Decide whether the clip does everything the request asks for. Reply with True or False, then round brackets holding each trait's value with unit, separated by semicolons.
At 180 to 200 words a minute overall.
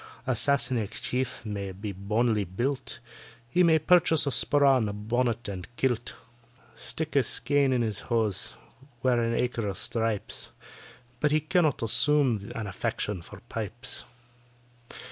False (135 wpm)